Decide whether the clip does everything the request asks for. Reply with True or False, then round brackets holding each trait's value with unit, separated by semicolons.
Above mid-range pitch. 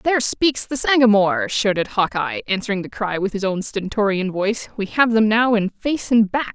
True (210 Hz)